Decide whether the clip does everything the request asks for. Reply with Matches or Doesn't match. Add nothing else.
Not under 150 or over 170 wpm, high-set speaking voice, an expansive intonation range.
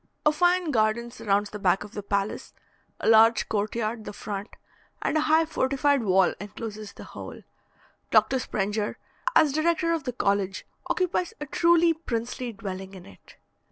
Matches